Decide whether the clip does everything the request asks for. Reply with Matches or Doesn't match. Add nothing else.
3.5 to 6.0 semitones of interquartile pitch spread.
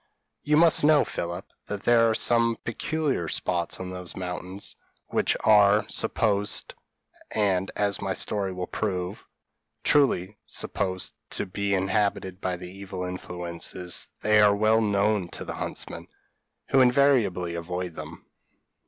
Doesn't match